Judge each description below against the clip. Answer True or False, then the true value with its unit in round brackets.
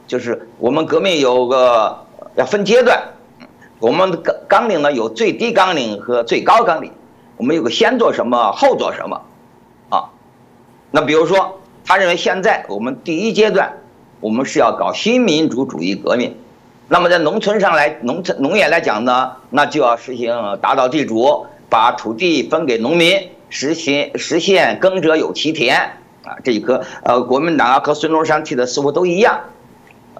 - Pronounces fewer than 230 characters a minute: False (250 characters per minute)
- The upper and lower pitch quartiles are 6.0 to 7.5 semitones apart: True (6.7 semitones)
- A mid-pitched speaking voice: True (155 Hz)